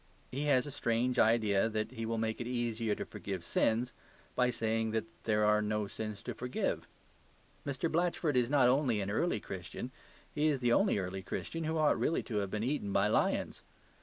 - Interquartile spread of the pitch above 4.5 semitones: No, average, 3.8 semitones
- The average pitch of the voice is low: Yes, low, 115 Hz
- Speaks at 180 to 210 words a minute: Yes, average, 195 wpm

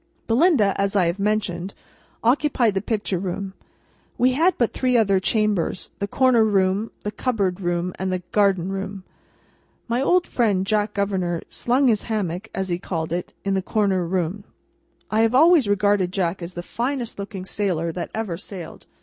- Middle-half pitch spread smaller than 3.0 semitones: No, average, 3.3 semitones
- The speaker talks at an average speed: Yes, average, 170 wpm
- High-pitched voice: Yes, high, 200 Hz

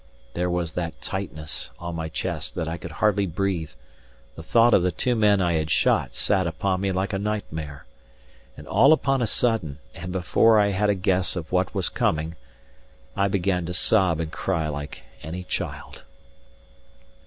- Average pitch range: Yes, average, 3.4 semitones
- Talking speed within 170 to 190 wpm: Yes, average, 175 wpm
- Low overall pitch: Yes, very low, 90 Hz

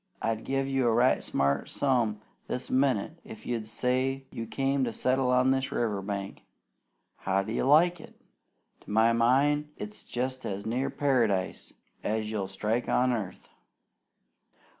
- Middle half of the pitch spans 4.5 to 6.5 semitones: No, average, 3.6 semitones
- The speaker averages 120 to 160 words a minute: Yes, average, 150 wpm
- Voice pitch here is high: No, low, 125 Hz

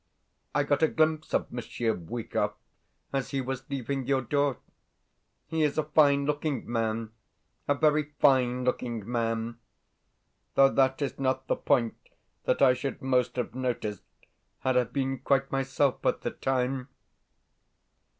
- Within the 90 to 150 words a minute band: Yes, average, 145 wpm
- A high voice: No, low, 130 Hz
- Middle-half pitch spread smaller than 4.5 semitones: Yes, narrow, 2.4 semitones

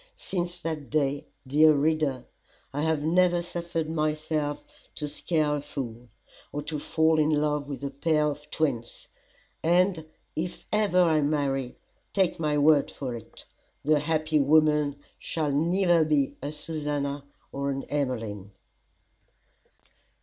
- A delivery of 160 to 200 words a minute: No, slow, 135 wpm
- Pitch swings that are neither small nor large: No, narrow, 2.1 semitones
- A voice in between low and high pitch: Yes, medium, 150 Hz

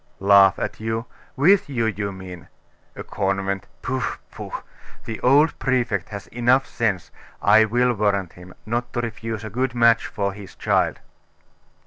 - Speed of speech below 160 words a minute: Yes, average, 150 wpm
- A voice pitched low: Yes, low, 110 Hz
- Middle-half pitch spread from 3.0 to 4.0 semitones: Yes, average, 3.7 semitones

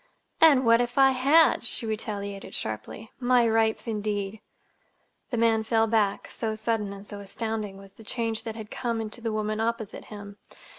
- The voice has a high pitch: Yes, high, 220 Hz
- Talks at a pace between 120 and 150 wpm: No, average, 170 wpm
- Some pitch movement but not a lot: No, narrow, 1.9 semitones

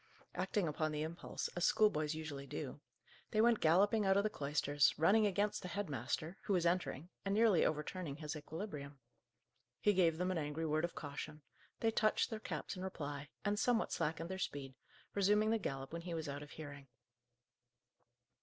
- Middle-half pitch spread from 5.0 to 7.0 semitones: Yes, average, 5.3 semitones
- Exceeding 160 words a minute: Yes, average, 180 wpm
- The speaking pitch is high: No, medium, 165 Hz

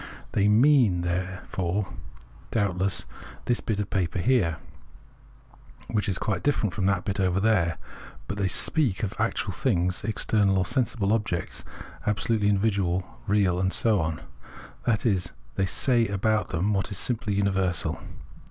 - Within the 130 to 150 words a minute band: Yes, average, 145 wpm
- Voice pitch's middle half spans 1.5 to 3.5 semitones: Yes, average, 2.9 semitones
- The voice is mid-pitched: No, low, 100 Hz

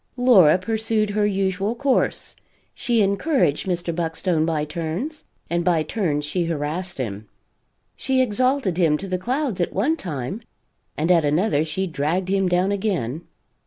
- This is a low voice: No, medium, 185 Hz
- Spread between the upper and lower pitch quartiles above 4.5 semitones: Yes, average, 5.0 semitones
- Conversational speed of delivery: Yes, average, 150 wpm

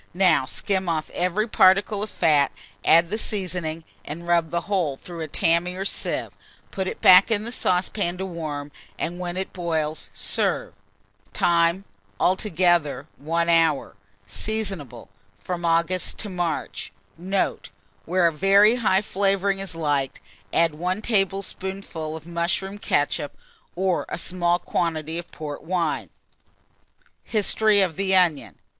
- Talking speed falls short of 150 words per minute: Yes, average, 140 wpm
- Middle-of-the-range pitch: Yes, medium, 175 Hz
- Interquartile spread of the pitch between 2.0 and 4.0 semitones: Yes, average, 3.0 semitones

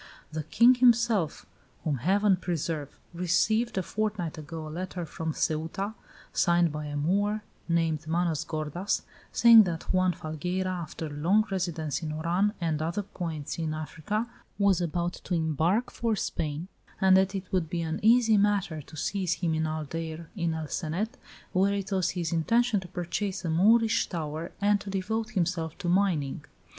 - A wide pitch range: No, average, 4.0 semitones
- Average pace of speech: Yes, average, 165 wpm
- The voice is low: No, medium, 175 Hz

